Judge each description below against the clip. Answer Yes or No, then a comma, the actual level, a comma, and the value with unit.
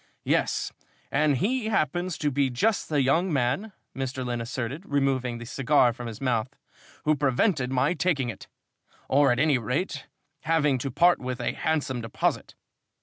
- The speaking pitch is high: No, low, 135 Hz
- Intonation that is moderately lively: Yes, average, 3.7 semitones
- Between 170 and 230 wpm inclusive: No, average, 160 wpm